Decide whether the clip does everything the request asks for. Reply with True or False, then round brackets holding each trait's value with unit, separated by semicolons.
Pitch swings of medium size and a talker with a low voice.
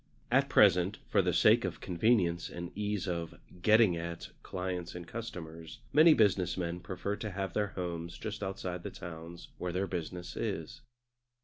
True (3.2 semitones; 90 Hz)